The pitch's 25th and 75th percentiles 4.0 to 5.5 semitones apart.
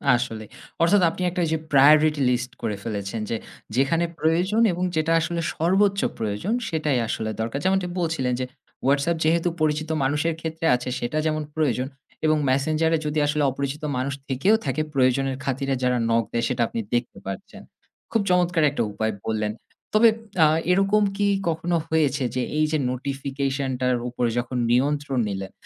Yes: average, 4.5 semitones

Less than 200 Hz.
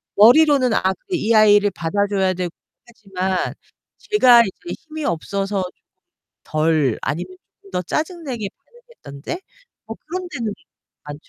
No: high, 205 Hz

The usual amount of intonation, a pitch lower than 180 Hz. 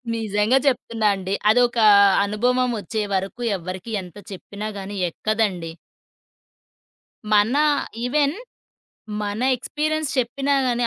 No: average, 3.7 semitones; high, 220 Hz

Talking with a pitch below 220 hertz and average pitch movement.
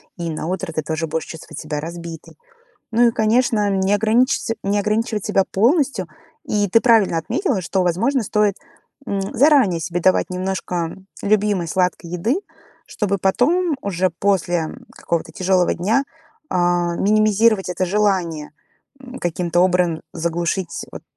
Yes: high, 190 Hz; average, 3.8 semitones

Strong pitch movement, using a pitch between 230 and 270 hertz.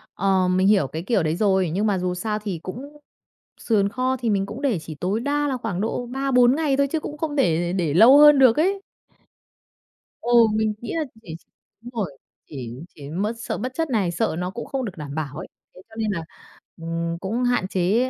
No: wide, 6.0 semitones; high, 215 Hz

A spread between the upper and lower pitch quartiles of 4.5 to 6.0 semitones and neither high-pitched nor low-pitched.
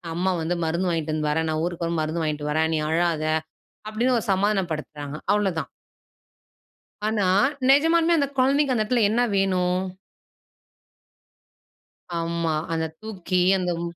Yes: average, 5.0 semitones; medium, 175 Hz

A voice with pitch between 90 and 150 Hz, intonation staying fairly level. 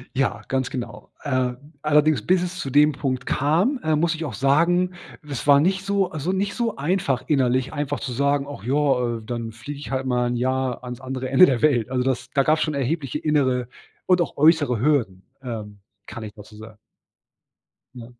No: low, 135 Hz; average, 3.6 semitones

